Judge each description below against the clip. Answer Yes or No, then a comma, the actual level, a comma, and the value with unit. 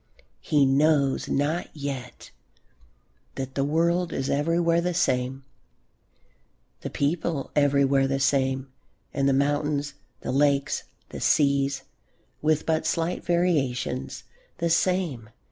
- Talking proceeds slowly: Yes, slow, 110 wpm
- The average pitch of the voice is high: No, medium, 140 Hz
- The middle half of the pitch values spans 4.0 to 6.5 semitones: No, average, 3.2 semitones